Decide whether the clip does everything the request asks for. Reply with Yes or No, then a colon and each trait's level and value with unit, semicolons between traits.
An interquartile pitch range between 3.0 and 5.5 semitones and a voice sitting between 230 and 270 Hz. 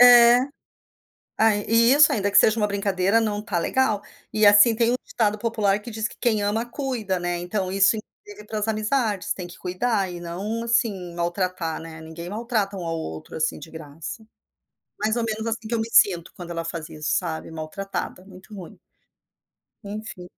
No: average, 4.0 semitones; high, 205 Hz